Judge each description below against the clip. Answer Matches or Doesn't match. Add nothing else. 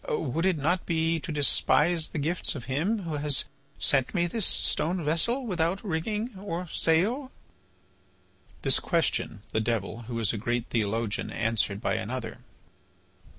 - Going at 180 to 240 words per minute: Doesn't match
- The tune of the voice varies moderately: Doesn't match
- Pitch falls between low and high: Matches